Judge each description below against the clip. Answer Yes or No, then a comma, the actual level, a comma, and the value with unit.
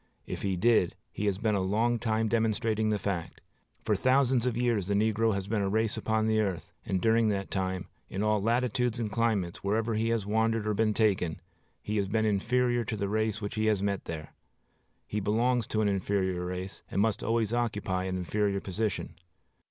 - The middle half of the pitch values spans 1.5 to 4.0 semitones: Yes, narrow, 2.4 semitones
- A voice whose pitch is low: Yes, low, 110 Hz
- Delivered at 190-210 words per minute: Yes, fast, 205 wpm